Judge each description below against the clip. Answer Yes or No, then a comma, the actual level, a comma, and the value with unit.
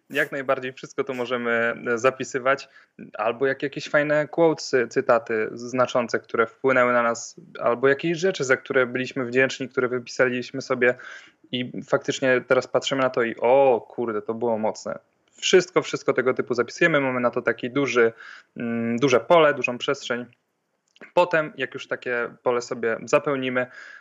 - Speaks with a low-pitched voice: Yes, low, 130 Hz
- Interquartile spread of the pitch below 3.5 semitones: Yes, narrow, 2.5 semitones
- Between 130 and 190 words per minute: Yes, average, 150 wpm